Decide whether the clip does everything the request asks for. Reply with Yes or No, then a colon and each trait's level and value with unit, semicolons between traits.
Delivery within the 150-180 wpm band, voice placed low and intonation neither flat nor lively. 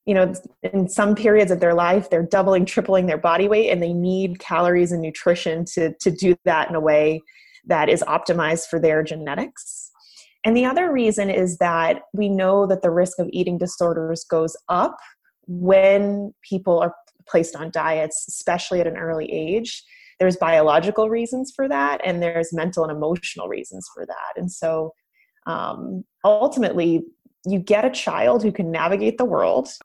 No: average, 175 wpm; medium, 180 Hz; average, 3.5 semitones